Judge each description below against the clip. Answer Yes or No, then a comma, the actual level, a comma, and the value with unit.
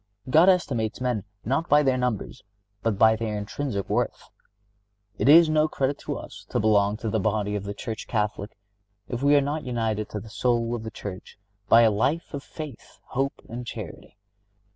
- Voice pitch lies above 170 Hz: No, low, 115 Hz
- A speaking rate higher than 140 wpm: Yes, average, 185 wpm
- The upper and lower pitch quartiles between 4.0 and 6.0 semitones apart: Yes, average, 4.5 semitones